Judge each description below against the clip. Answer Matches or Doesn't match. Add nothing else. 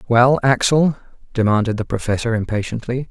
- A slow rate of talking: Matches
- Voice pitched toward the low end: Matches